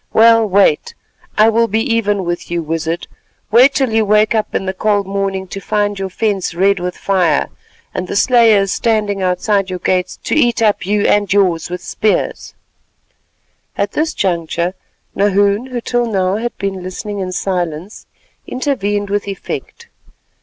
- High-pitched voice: Yes, high, 200 Hz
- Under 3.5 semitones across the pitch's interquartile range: Yes, average, 2.8 semitones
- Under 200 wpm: Yes, average, 160 wpm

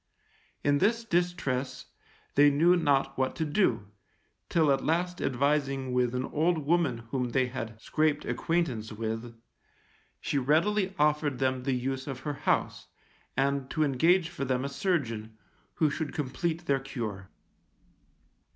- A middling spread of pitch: Yes, average, 4.0 semitones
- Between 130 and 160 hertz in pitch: Yes, medium, 140 Hz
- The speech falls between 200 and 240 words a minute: No, average, 140 wpm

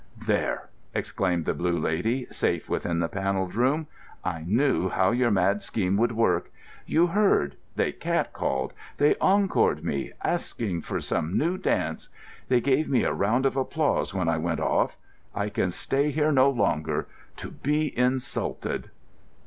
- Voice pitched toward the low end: Yes, low, 115 Hz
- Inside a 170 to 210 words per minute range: No, average, 155 wpm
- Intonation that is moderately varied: No, wide, 7.4 semitones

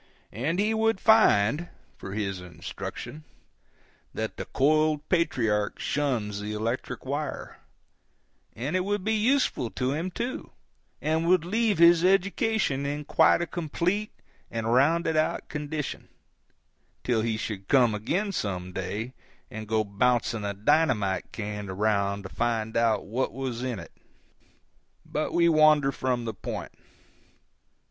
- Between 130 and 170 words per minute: Yes, average, 140 wpm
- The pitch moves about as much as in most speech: No, wide, 7.6 semitones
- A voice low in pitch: Yes, low, 130 Hz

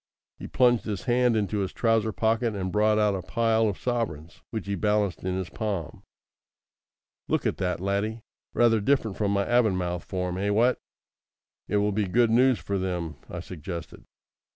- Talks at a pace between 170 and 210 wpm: Yes, average, 175 wpm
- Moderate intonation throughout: Yes, average, 3.3 semitones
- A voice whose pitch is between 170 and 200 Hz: No, low, 105 Hz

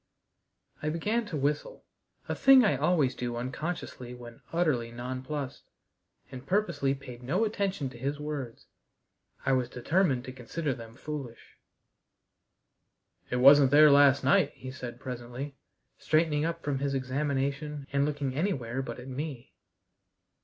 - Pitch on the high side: No, medium, 140 Hz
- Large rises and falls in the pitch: No, average, 3.1 semitones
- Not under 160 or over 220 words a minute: No, average, 140 wpm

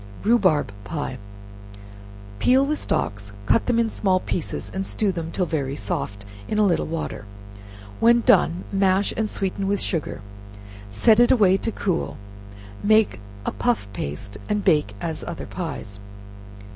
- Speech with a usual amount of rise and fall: No, wide, 6.4 semitones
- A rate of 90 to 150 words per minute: Yes, average, 145 wpm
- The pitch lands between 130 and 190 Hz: Yes, medium, 185 Hz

